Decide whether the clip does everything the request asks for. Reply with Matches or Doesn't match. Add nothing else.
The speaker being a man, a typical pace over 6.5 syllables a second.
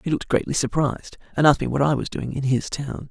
Matches